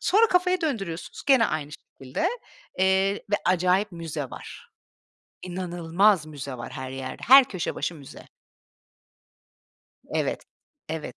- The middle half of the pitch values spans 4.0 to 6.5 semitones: Yes, average, 5.3 semitones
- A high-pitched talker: No, medium, 180 Hz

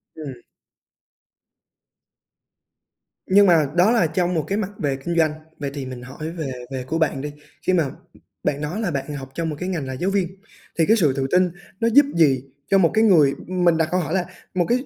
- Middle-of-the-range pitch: Yes, medium, 165 Hz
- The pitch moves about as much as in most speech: Yes, average, 4.4 semitones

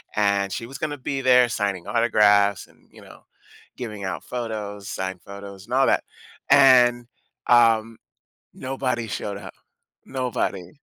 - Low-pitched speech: Yes, low, 115 Hz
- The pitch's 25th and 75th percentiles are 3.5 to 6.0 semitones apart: Yes, average, 3.8 semitones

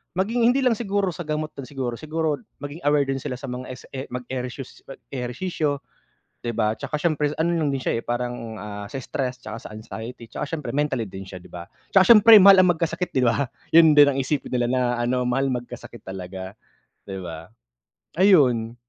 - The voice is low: Yes, low, 130 Hz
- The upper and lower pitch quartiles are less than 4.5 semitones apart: No, average, 4.8 semitones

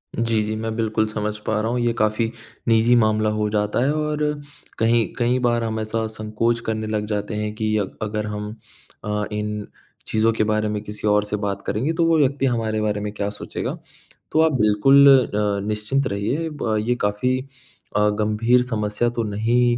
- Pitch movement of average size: No, narrow, 2.0 semitones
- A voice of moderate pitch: No, low, 110 Hz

